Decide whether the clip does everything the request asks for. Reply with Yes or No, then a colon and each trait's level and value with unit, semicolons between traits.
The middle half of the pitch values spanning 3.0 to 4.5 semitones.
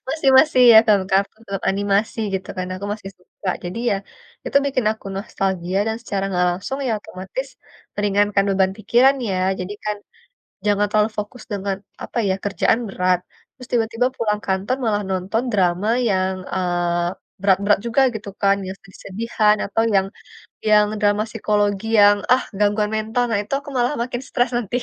No: narrow, 2.6 semitones